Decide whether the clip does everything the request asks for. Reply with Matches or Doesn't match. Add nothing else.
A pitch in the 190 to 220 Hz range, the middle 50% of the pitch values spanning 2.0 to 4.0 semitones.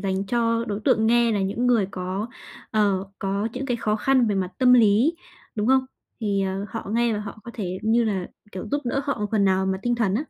Matches